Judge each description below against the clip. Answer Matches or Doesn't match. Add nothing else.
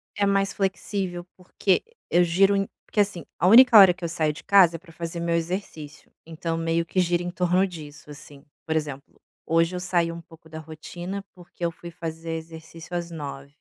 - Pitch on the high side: Doesn't match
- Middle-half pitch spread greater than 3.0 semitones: Doesn't match